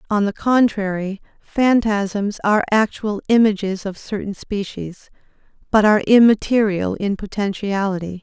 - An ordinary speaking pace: No, slow, 110 wpm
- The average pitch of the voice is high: Yes, high, 205 Hz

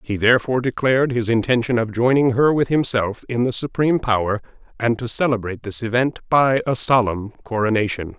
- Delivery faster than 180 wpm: No, average, 170 wpm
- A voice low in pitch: Yes, low, 120 Hz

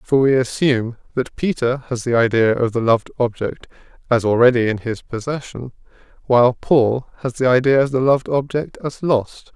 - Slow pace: No, average, 175 wpm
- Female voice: No, male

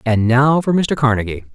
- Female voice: No, male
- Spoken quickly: No, average, 195 wpm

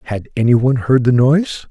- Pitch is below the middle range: Yes, low, 125 Hz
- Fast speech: Yes, fast, 210 wpm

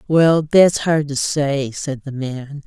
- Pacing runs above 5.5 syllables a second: No, 3.3 syllables/s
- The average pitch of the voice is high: No, medium, 145 Hz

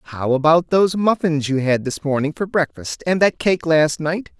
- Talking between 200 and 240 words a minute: Yes, fast, 205 wpm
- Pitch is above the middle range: No, medium, 155 Hz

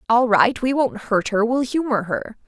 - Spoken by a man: No, female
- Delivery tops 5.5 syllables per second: No, 4.5 syllables/s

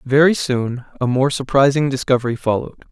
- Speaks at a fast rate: No, average, 145 wpm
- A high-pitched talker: No, low, 135 Hz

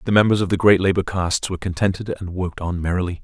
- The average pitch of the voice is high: No, very low, 95 Hz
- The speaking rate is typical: No, fast, 240 wpm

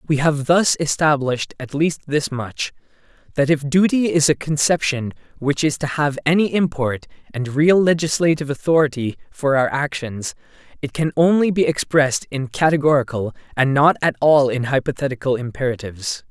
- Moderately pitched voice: Yes, medium, 145 Hz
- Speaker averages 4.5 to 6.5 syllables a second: Yes, 5.2 syllables/s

